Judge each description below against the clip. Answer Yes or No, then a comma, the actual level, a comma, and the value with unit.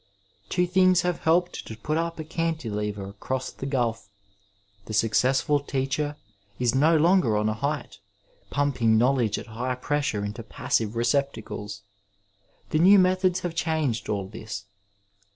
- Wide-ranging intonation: Yes, wide, 6.5 semitones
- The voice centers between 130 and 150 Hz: Yes, low, 135 Hz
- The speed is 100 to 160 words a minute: Yes, average, 145 wpm